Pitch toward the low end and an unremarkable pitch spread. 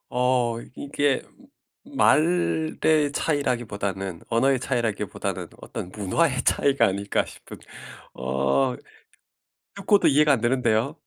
No: low, 125 Hz; wide, 6.0 semitones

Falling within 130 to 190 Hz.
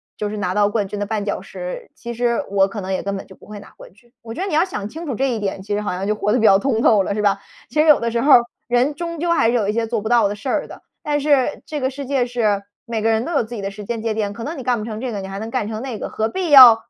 No: high, 225 Hz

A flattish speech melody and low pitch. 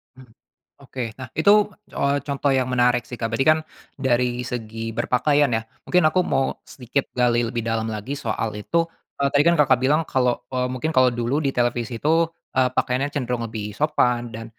No: average, 3.1 semitones; low, 125 Hz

